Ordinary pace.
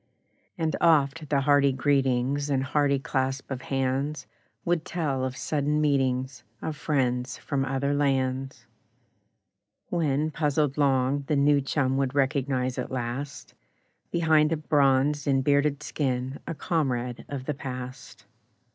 No: slow, 130 wpm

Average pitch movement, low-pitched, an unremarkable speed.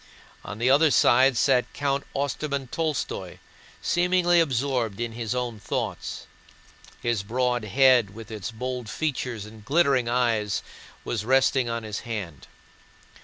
No: average, 3.5 semitones; low, 125 Hz; slow, 130 wpm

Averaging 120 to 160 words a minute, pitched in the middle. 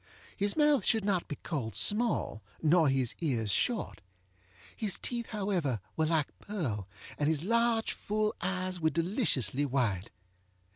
Yes: average, 140 wpm; medium, 170 Hz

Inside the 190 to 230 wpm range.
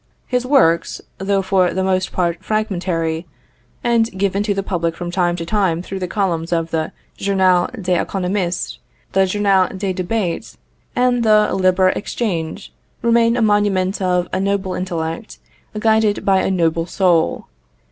No: average, 150 wpm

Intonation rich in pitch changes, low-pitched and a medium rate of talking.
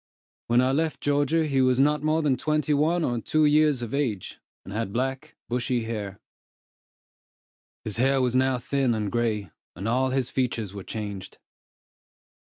No: average, 4.2 semitones; low, 130 Hz; average, 160 wpm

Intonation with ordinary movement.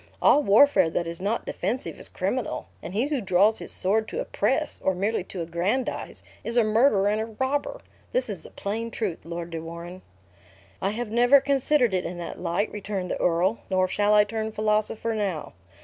Yes: average, 4.1 semitones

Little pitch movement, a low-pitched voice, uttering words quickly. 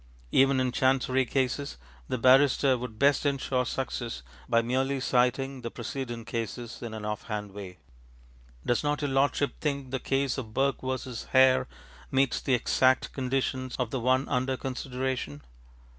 No: narrow, 2.0 semitones; low, 130 Hz; average, 160 wpm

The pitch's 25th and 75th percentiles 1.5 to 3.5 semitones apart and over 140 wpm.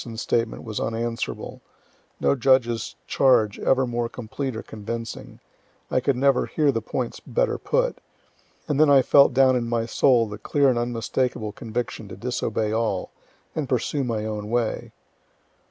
Yes: average, 2.8 semitones; average, 155 wpm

